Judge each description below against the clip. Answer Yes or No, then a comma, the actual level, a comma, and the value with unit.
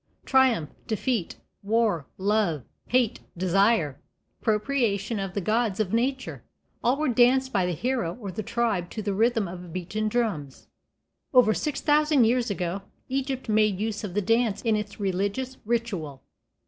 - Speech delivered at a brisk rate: No, average, 150 wpm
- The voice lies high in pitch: Yes, high, 215 Hz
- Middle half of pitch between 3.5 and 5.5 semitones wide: Yes, average, 4.0 semitones